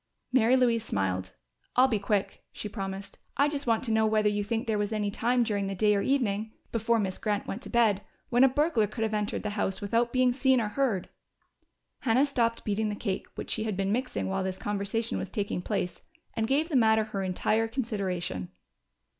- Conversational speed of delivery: No, fast, 210 wpm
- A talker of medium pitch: No, high, 220 Hz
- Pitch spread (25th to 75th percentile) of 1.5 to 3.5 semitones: Yes, average, 2.9 semitones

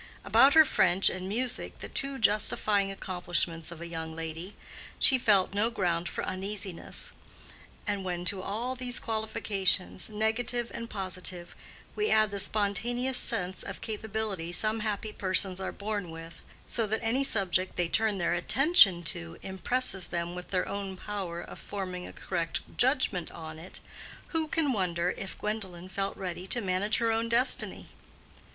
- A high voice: Yes, high, 195 Hz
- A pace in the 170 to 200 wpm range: No, average, 160 wpm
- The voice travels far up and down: No, average, 3.6 semitones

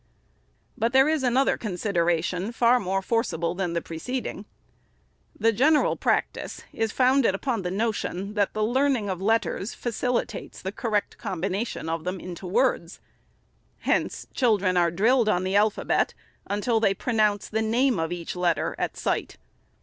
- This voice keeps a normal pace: Yes, average, 150 wpm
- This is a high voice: Yes, high, 205 Hz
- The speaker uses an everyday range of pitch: Yes, average, 4.6 semitones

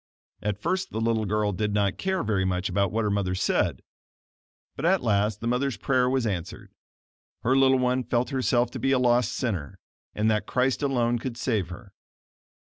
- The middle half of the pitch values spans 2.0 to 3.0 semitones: No, average, 3.8 semitones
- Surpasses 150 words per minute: Yes, average, 190 wpm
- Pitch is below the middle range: Yes, low, 115 Hz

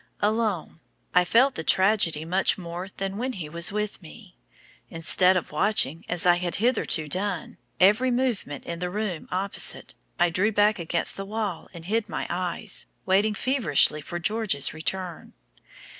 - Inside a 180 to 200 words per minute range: No, average, 160 wpm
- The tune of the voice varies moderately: Yes, average, 3.8 semitones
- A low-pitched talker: No, medium, 185 Hz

